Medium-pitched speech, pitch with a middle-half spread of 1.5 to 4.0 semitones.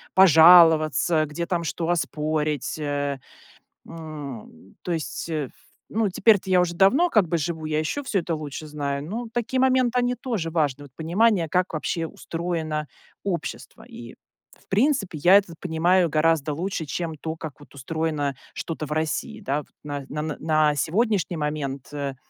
Yes: medium, 160 Hz; average, 3.5 semitones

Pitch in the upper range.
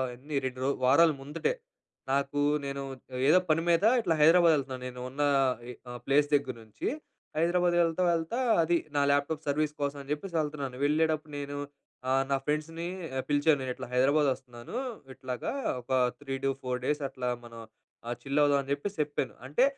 No: medium, 145 Hz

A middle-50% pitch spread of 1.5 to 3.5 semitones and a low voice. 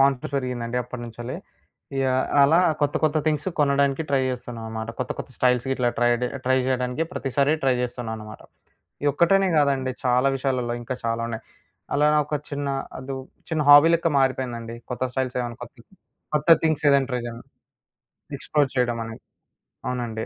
Yes: average, 2.7 semitones; low, 130 Hz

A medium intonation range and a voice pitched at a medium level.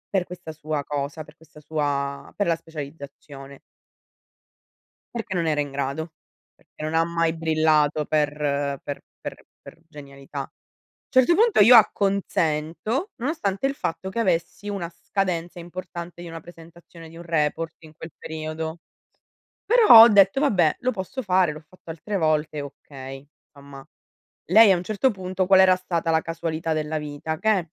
Yes: average, 3.7 semitones; medium, 165 Hz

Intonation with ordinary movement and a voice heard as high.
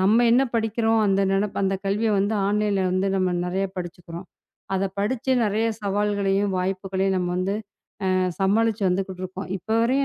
No: narrow, 2.0 semitones; high, 195 Hz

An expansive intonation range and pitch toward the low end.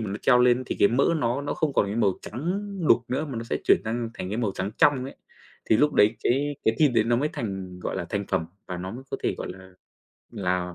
No: average, 4.9 semitones; low, 115 Hz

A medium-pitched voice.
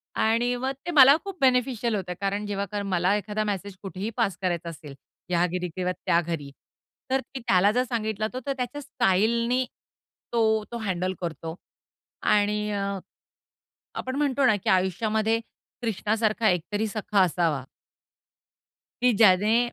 No: high, 210 Hz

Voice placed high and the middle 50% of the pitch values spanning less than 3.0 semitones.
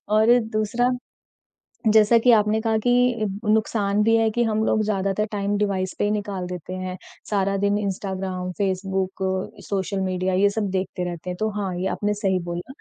Yes: high, 200 Hz; narrow, 2.5 semitones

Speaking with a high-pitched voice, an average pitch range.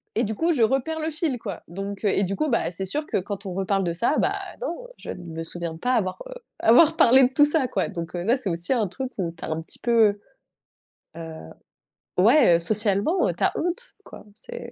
No: high, 215 Hz; wide, 7.6 semitones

